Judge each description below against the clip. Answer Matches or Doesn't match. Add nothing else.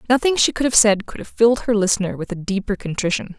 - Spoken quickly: Matches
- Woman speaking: Matches